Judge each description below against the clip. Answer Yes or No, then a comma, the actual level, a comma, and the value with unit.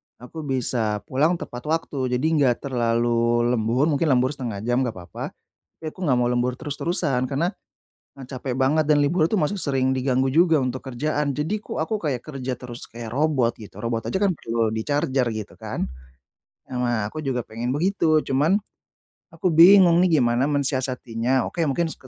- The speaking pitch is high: No, low, 130 Hz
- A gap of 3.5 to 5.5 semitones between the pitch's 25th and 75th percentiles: Yes, average, 4.1 semitones